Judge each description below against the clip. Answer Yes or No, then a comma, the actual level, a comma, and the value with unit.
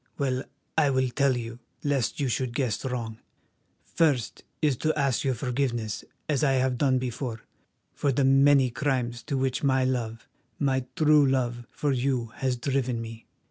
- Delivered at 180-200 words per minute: No, average, 170 wpm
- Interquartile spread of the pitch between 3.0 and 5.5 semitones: No, narrow, 2.5 semitones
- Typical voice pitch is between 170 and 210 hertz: No, low, 130 Hz